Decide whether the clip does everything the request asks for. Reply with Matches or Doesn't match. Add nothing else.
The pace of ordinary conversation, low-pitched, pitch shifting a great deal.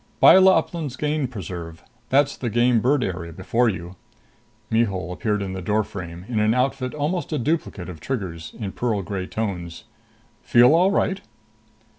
Matches